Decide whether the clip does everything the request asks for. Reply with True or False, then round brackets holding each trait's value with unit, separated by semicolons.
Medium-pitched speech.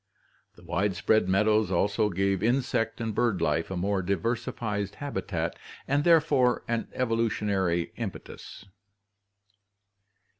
False (105 Hz)